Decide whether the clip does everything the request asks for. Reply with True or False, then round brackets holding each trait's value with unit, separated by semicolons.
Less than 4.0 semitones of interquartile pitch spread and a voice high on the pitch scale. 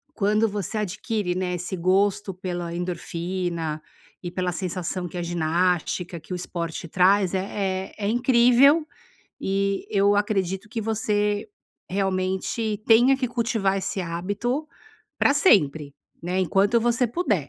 True (3.3 semitones; 195 Hz)